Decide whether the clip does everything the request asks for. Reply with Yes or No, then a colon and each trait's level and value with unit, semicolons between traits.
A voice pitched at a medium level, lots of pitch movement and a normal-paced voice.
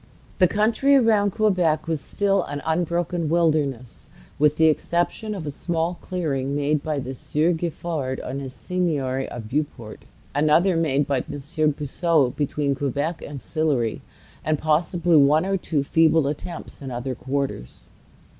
No: medium, 155 Hz; average, 3.7 semitones; average, 150 wpm